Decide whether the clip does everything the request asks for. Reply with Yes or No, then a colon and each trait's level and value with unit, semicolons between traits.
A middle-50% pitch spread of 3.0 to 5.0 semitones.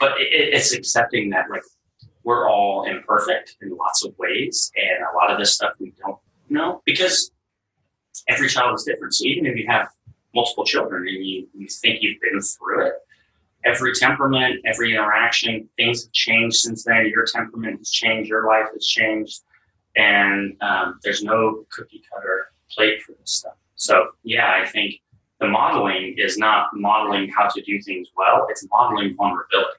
No: narrow, 2.5 semitones